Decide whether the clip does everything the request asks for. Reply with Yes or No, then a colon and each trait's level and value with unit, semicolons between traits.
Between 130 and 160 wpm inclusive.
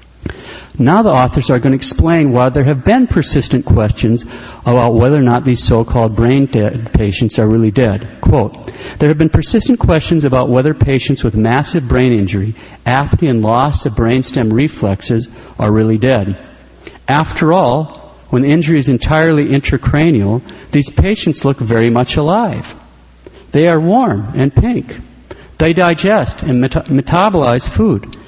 Yes: average, 155 wpm